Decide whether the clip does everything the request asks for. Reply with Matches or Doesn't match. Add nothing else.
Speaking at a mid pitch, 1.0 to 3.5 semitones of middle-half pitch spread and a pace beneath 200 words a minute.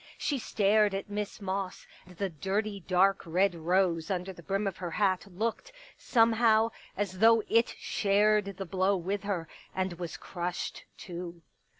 Doesn't match